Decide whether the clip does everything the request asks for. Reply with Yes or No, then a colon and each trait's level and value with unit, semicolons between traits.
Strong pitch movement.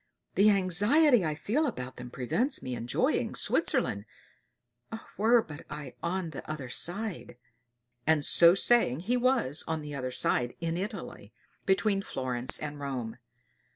Yes: wide, 8.1 semitones